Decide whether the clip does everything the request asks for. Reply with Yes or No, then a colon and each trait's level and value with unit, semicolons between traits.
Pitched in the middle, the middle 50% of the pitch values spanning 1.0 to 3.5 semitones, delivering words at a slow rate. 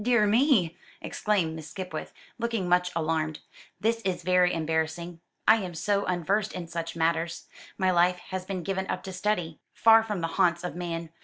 No: medium, 180 Hz; average, 3.2 semitones; average, 175 wpm